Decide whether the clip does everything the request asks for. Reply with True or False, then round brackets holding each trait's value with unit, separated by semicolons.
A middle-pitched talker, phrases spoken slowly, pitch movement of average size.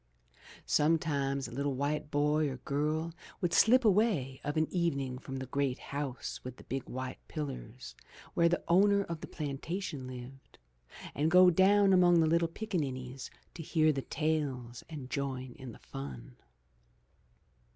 False (145 Hz; 160 wpm; 4.2 semitones)